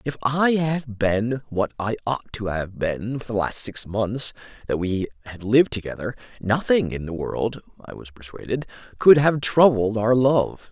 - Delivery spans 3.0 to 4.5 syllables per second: Yes, 4.3 syllables/s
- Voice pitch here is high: No, low, 115 Hz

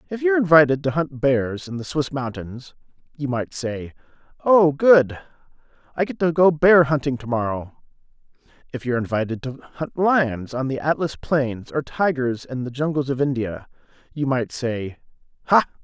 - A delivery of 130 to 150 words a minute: No, average, 165 wpm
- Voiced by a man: Yes, male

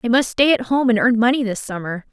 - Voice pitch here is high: Yes, high, 235 Hz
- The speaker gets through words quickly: Yes, fast, 285 wpm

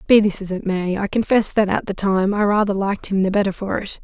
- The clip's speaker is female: Yes, female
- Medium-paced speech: No, fast, 285 wpm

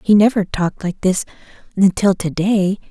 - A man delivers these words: No, female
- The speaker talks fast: No, average, 165 wpm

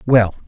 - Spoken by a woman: No, male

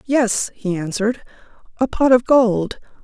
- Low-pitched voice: No, high, 230 Hz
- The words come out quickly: No, average, 140 wpm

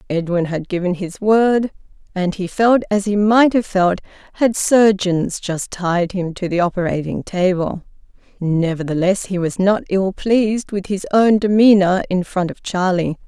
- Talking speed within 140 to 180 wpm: Yes, average, 165 wpm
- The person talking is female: Yes, female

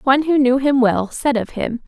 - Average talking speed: No, fast, 255 wpm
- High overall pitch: Yes, very high, 265 Hz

